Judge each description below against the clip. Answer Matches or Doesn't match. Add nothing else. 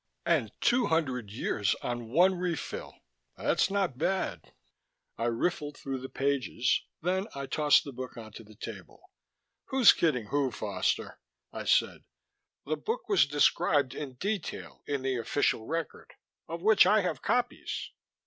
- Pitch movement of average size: Doesn't match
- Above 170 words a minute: Doesn't match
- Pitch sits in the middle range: Matches